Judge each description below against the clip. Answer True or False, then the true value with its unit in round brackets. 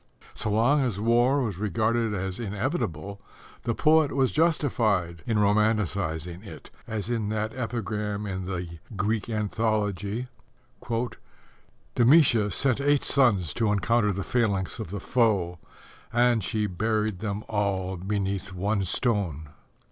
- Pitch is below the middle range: True (105 Hz)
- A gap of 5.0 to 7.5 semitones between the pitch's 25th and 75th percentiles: False (3.3 semitones)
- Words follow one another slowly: True (125 wpm)